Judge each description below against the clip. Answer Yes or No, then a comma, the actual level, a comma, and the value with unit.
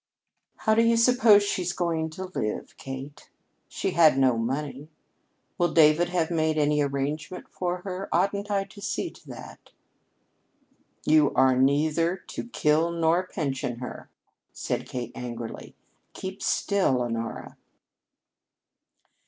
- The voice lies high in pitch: No, medium, 160 Hz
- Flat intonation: No, average, 5.2 semitones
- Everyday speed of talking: No, slow, 130 wpm